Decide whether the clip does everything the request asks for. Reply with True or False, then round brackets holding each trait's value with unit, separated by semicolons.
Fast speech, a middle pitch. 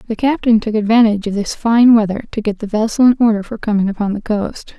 False (240 wpm; 220 Hz)